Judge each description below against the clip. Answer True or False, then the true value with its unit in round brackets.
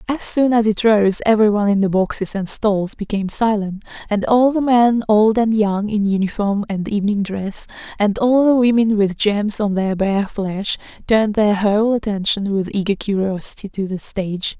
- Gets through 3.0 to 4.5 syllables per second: False (4.9 syllables/s)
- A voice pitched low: False (210 Hz)